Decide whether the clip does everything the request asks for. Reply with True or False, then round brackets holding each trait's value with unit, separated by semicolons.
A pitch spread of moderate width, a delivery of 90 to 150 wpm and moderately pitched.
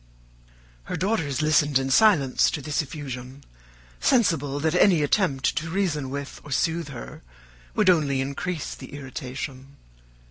True (3.5 semitones; 135 wpm; 145 Hz)